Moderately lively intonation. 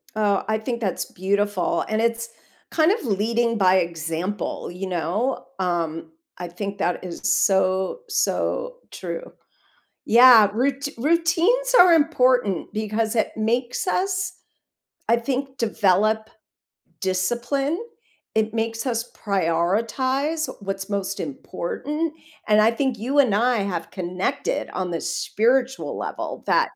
No: wide, 5.7 semitones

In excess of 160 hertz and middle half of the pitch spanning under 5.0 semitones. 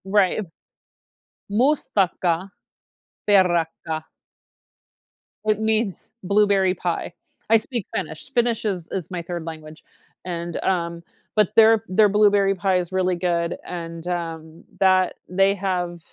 Yes: medium, 185 Hz; average, 3.3 semitones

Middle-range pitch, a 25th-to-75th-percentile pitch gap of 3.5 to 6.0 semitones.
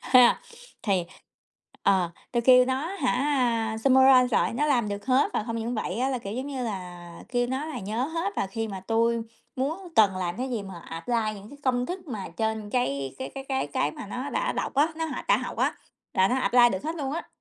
No: high, 245 Hz; average, 4.7 semitones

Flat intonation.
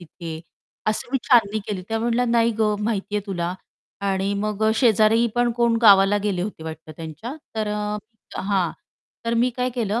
No: average, 3.1 semitones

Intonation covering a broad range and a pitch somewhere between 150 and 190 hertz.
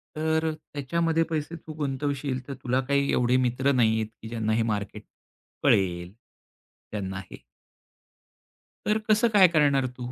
No: wide, 5.7 semitones; low, 135 Hz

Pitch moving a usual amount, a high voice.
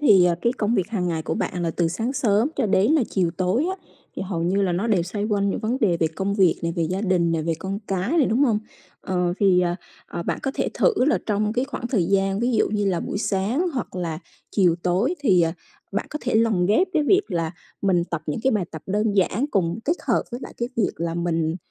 Yes: average, 4.5 semitones; high, 195 Hz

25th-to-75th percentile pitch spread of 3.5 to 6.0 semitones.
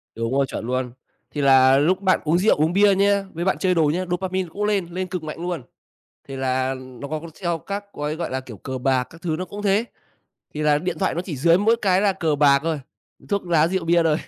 Yes: average, 5.1 semitones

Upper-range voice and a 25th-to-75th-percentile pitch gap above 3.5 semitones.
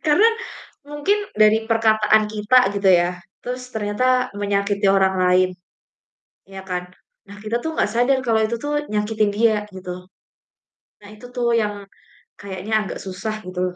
No: high, 215 Hz; average, 3.2 semitones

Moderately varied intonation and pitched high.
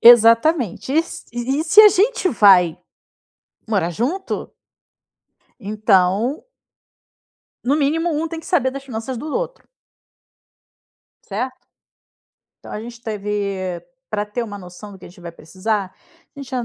No: wide, 6.3 semitones; high, 230 Hz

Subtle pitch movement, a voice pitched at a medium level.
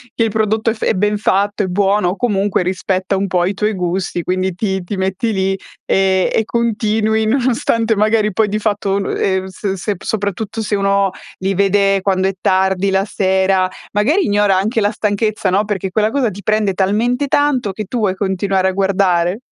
No: narrow, 2.2 semitones; high, 200 Hz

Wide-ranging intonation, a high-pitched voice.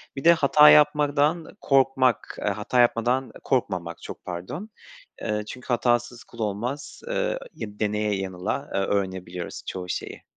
No: wide, 6.1 semitones; low, 120 Hz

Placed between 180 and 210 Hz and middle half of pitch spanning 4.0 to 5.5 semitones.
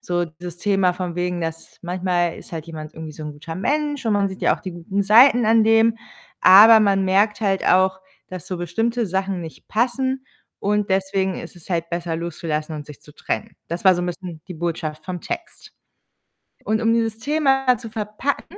Yes: high, 190 Hz; average, 4.6 semitones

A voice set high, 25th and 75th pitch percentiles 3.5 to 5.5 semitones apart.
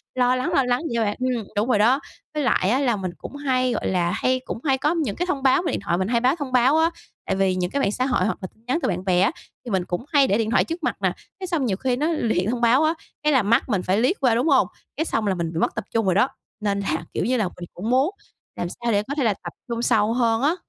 Yes: high, 235 Hz; average, 4.7 semitones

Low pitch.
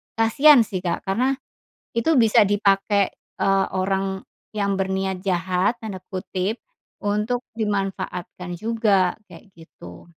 No: high, 195 Hz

